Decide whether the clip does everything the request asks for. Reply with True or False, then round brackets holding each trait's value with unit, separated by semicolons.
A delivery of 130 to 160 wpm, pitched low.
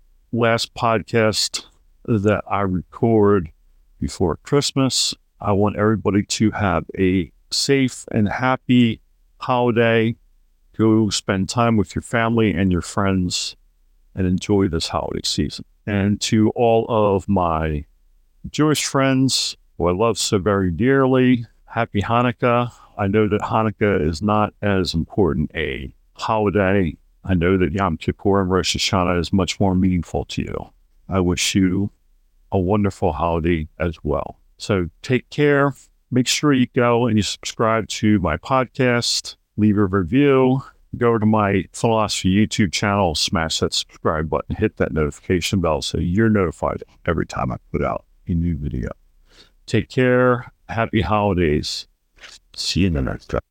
True (145 wpm; 100 Hz)